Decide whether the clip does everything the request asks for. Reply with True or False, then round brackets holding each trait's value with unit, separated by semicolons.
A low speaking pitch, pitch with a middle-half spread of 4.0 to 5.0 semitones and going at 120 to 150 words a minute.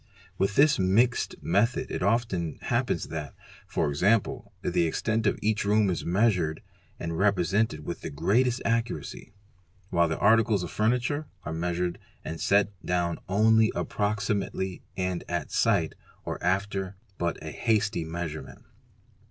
True (100 Hz; 4.3 semitones; 135 wpm)